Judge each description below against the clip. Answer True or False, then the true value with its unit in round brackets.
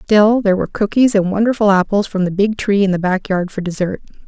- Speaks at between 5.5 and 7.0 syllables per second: True (6.1 syllables/s)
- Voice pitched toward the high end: True (200 Hz)